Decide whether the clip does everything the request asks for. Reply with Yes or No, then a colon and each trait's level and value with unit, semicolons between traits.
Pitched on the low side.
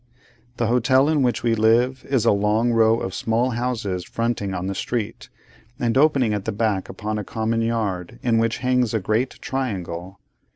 Yes: low, 115 Hz